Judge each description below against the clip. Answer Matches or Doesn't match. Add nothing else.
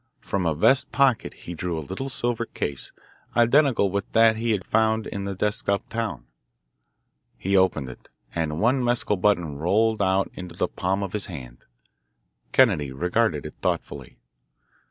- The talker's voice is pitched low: Matches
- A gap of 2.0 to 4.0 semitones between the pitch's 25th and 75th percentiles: Doesn't match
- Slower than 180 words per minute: Matches